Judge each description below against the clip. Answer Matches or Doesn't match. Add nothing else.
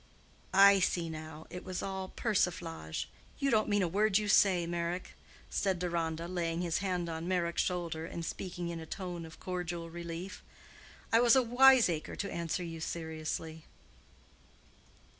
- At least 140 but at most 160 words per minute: Matches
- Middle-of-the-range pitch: Matches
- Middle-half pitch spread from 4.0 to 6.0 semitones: Doesn't match